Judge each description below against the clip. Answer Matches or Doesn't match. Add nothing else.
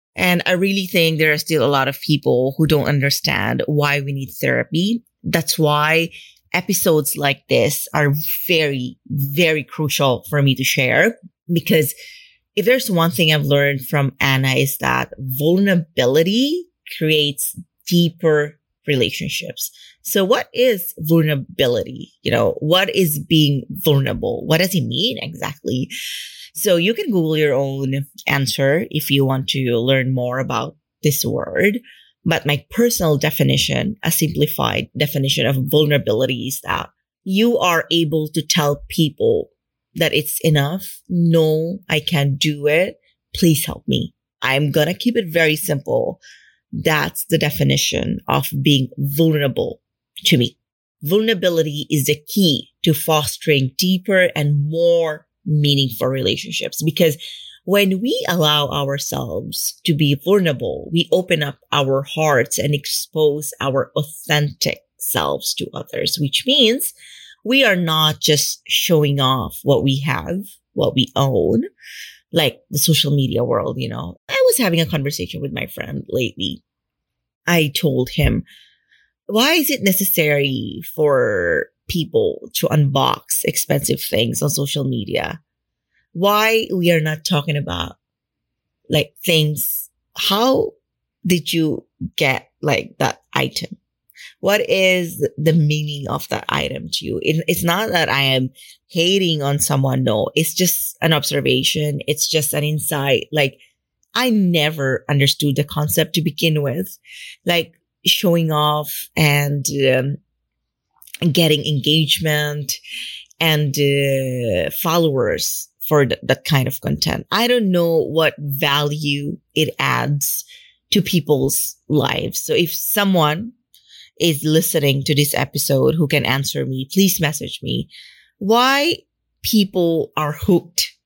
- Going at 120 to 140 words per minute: Matches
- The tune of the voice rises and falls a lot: Doesn't match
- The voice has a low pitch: Doesn't match